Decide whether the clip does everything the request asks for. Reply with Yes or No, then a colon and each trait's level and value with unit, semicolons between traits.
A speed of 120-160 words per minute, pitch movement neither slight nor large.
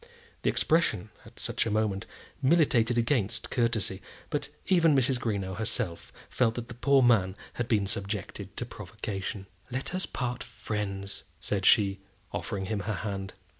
Yes: average, 150 wpm; average, 3.9 semitones